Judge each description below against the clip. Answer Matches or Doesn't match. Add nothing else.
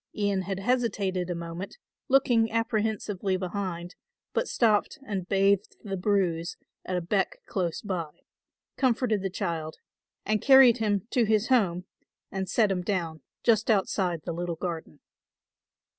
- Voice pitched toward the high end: Matches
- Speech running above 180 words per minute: Doesn't match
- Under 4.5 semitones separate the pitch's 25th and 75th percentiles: Matches